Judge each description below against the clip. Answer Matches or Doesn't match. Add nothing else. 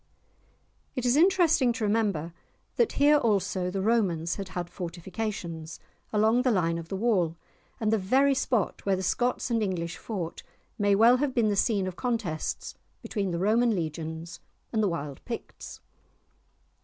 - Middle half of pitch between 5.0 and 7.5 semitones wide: Matches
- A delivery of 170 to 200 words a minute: Doesn't match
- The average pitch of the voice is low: Doesn't match